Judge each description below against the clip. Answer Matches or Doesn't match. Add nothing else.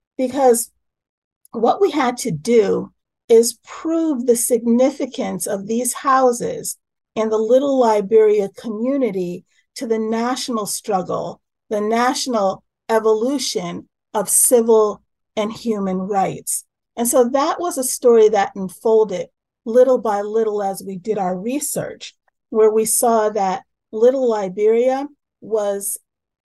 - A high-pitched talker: Matches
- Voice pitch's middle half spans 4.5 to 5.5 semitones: Doesn't match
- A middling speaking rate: Doesn't match